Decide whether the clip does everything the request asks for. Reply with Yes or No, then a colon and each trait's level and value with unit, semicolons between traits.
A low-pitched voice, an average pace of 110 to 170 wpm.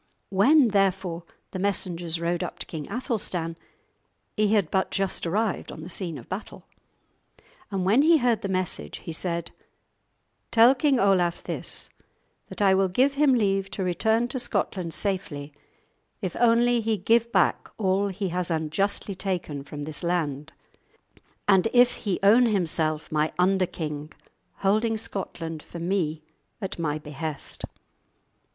No: high, 190 Hz; average, 150 wpm